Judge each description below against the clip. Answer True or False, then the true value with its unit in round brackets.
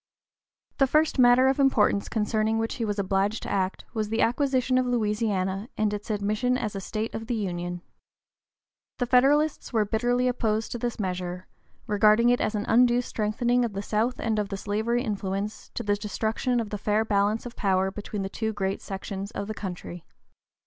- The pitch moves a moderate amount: True (3.2 semitones)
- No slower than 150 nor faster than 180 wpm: False (190 wpm)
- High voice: True (215 Hz)